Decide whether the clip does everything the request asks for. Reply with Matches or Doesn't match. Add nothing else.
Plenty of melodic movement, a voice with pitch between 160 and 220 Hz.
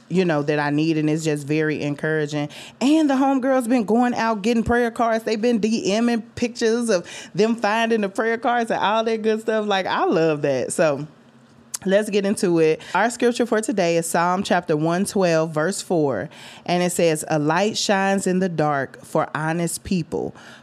Matches